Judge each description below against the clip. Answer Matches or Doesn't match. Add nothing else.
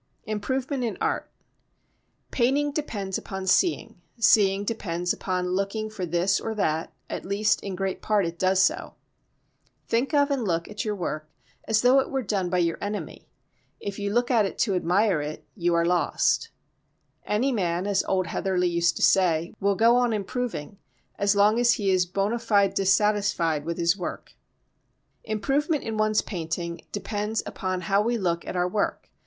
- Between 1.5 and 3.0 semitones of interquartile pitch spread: Doesn't match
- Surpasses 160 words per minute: Matches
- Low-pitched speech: Doesn't match